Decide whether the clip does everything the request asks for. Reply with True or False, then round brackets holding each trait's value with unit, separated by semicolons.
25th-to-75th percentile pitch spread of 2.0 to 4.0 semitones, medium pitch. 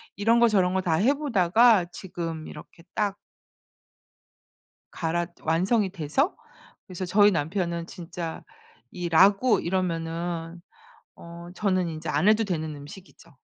True (3.5 semitones; 180 Hz)